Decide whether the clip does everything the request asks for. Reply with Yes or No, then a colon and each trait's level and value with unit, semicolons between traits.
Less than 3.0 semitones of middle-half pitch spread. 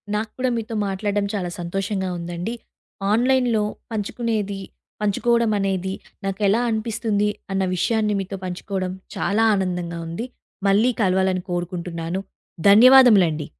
No: average, 3.3 semitones